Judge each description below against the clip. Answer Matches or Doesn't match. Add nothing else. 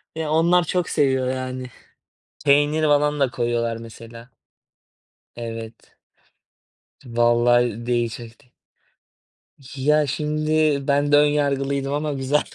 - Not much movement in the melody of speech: Doesn't match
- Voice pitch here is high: Doesn't match